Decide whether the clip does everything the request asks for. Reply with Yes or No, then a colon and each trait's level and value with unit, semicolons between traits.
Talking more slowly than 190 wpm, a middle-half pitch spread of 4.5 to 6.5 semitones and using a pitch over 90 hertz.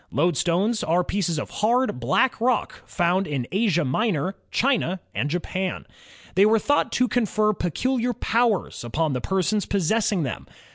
Yes: average, 145 wpm; average, 5.1 semitones; high, 190 Hz